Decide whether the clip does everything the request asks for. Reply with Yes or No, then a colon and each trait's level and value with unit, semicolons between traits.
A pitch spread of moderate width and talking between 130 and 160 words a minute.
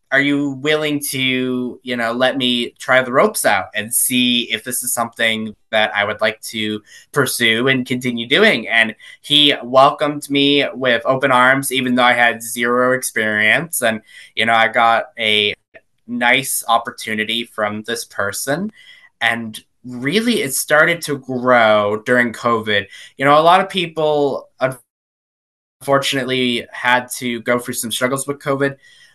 Yes: average, 3.3 semitones; average, 150 wpm